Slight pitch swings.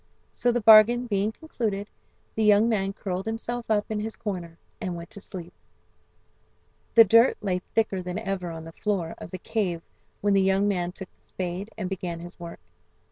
No: average, 3.4 semitones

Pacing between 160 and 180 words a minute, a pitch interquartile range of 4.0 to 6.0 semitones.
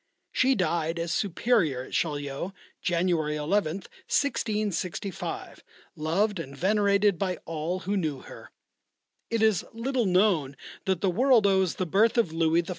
No: average, 140 wpm; average, 4.3 semitones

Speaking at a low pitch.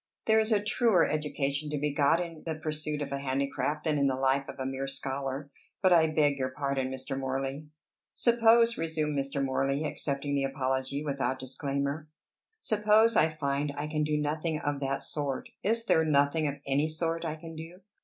No: medium, 145 Hz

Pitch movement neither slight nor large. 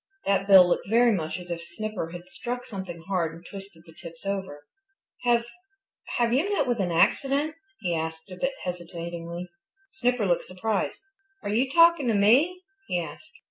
No: wide, 5.9 semitones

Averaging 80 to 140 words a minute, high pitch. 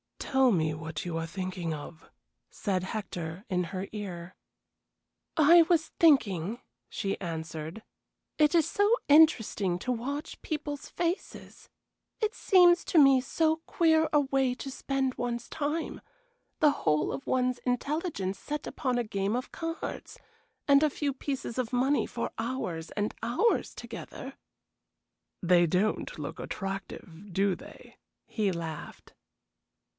Yes: slow, 135 wpm; high, 240 Hz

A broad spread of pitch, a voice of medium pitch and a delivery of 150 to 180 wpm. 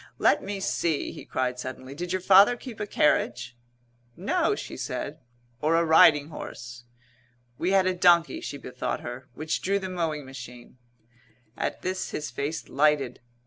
Yes: wide, 6.0 semitones; medium, 155 Hz; average, 160 wpm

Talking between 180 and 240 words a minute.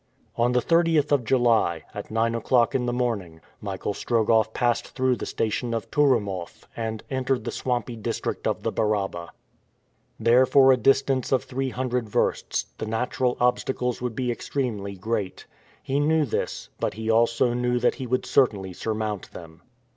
No: average, 165 wpm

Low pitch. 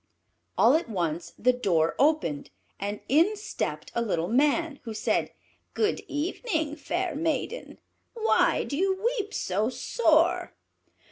No: very high, 300 Hz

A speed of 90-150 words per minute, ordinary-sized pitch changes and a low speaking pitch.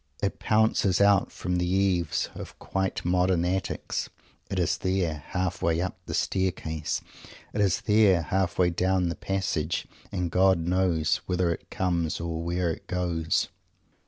No: average, 145 wpm; narrow, 2.0 semitones; very low, 90 Hz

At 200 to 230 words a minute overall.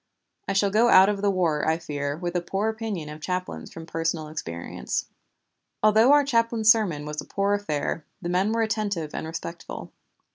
No: average, 185 wpm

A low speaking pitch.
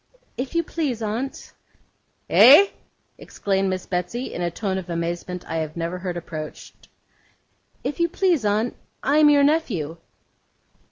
No: high, 205 Hz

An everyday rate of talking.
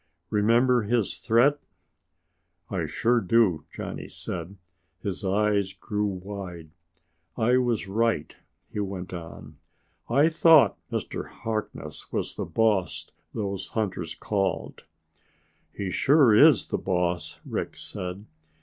No: slow, 115 wpm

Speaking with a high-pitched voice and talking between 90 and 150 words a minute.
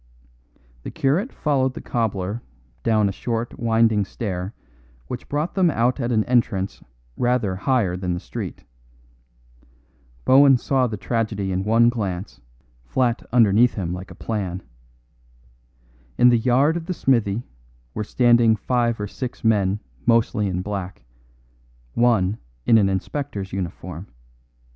No: low, 115 Hz; slow, 135 wpm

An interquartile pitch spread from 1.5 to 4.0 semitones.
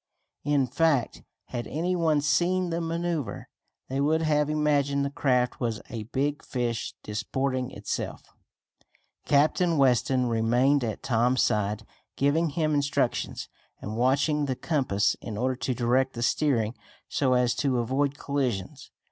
Yes: average, 3.5 semitones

